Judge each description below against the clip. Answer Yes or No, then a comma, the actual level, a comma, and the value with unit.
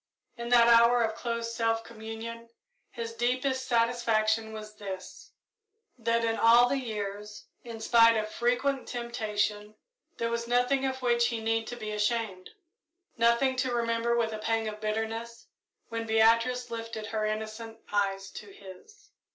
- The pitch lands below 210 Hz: No, high, 230 Hz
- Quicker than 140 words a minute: Yes, average, 150 wpm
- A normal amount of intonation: No, narrow, 1.5 semitones